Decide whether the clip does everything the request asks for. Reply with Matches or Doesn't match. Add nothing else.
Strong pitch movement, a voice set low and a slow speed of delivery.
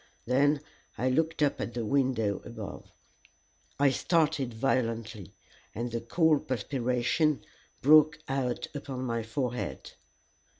Doesn't match